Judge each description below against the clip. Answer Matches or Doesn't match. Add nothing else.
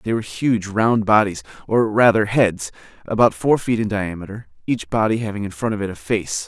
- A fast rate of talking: Doesn't match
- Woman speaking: Doesn't match